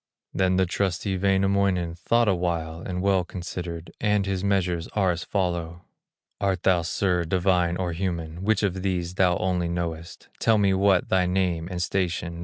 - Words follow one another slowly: No, average, 165 wpm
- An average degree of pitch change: No, narrow, 2.0 semitones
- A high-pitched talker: No, very low, 90 Hz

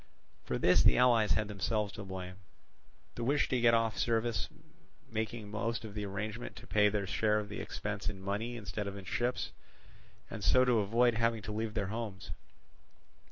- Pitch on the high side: No, low, 110 Hz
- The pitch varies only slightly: Yes, narrow, 2.3 semitones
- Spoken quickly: No, average, 185 wpm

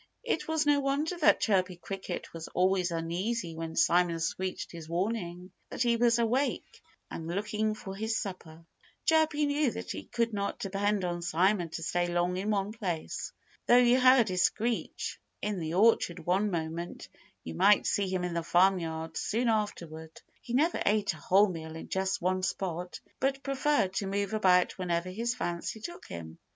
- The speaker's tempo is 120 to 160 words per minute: No, average, 175 wpm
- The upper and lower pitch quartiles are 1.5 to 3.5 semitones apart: No, average, 4.7 semitones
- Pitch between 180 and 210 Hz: Yes, high, 190 Hz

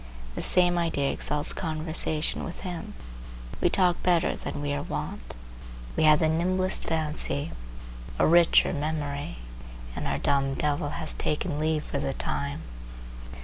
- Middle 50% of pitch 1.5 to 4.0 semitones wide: Yes, average, 2.9 semitones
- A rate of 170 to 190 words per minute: No, average, 145 wpm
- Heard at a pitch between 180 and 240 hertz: No, medium, 155 Hz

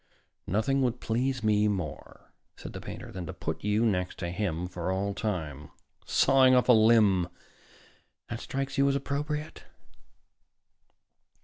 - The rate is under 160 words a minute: Yes, average, 140 wpm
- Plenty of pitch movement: Yes, wide, 5.9 semitones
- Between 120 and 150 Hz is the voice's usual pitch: No, low, 105 Hz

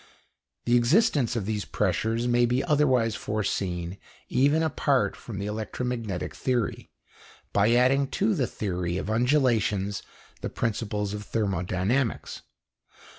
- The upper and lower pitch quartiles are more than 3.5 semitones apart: Yes, average, 4.0 semitones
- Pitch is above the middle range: No, low, 115 Hz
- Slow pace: Yes, slow, 120 wpm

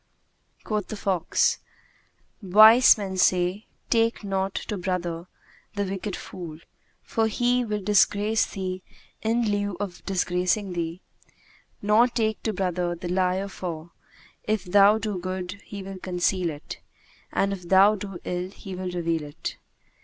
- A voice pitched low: No, high, 190 Hz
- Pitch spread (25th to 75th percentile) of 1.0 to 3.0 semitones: Yes, narrow, 2.6 semitones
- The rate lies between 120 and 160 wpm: Yes, average, 140 wpm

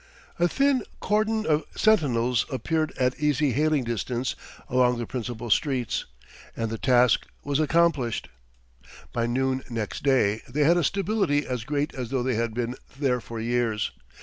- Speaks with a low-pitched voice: Yes, low, 130 Hz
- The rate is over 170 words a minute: No, average, 155 wpm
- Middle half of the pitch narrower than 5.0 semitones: Yes, average, 4.1 semitones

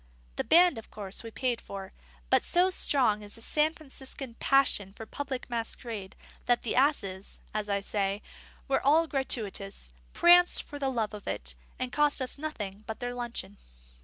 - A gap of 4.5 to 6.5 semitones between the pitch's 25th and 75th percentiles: Yes, wide, 5.4 semitones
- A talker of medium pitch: No, high, 240 Hz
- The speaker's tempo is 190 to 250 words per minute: No, average, 170 wpm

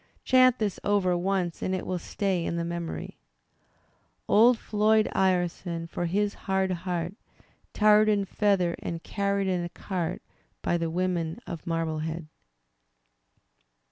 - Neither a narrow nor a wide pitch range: Yes, average, 3.0 semitones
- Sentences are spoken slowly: Yes, slow, 130 wpm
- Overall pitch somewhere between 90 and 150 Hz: No, medium, 185 Hz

